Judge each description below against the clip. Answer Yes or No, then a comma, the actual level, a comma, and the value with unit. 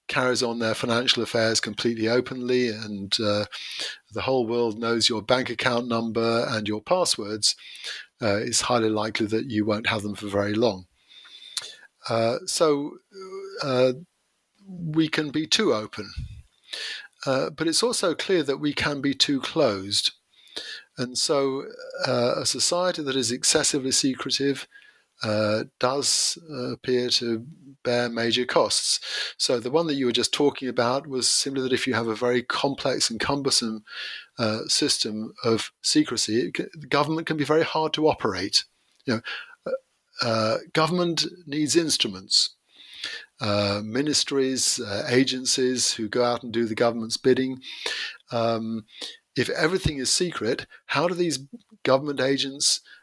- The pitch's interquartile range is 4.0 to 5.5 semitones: Yes, average, 4.6 semitones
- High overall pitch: No, low, 125 Hz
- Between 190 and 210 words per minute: No, average, 150 wpm